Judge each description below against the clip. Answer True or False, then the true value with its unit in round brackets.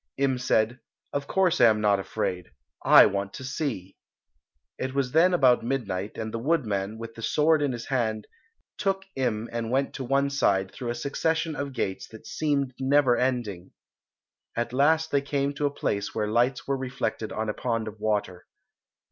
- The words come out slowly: False (180 wpm)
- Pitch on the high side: False (125 Hz)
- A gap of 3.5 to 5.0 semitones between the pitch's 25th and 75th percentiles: True (4.4 semitones)